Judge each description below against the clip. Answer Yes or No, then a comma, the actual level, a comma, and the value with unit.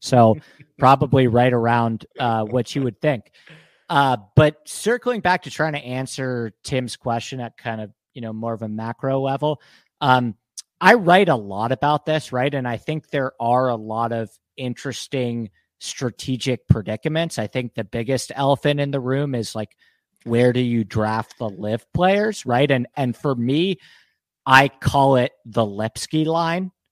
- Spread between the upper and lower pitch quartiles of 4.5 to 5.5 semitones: No, average, 3.7 semitones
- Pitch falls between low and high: No, low, 130 Hz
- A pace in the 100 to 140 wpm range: No, average, 170 wpm